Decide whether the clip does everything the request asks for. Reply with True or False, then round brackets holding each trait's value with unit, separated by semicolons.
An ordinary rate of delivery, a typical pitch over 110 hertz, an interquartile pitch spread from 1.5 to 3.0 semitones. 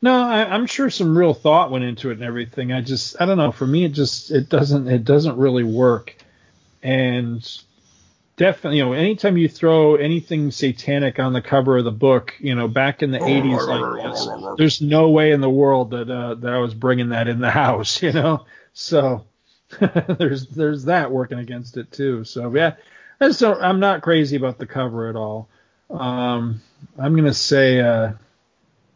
False (190 wpm; 135 Hz; 4.3 semitones)